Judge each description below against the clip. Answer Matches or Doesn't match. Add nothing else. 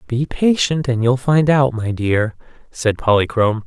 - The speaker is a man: Matches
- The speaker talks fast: Doesn't match